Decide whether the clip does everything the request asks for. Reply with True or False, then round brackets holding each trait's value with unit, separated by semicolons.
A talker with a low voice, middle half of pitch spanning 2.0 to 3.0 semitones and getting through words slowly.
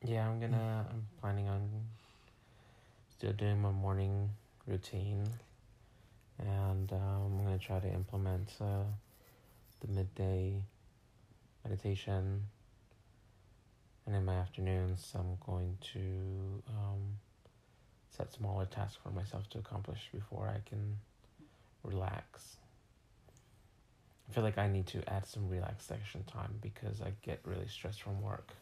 True (105 Hz; 2.5 semitones; 120 wpm)